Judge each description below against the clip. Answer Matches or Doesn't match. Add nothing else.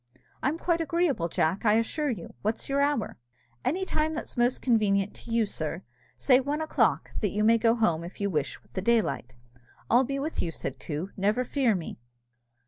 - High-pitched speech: Matches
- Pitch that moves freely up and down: Matches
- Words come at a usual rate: Matches